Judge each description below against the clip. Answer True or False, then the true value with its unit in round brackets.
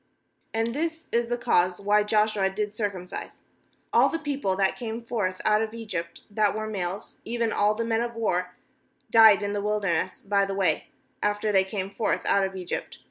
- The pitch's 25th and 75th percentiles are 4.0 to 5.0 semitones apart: False (2.7 semitones)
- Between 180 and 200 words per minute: True (190 wpm)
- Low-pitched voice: False (210 Hz)